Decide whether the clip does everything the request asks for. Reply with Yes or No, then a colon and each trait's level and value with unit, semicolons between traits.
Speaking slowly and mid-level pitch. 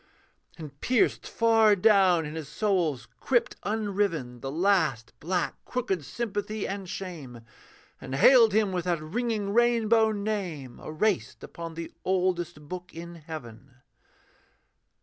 Yes: slow, 125 wpm; medium, 180 Hz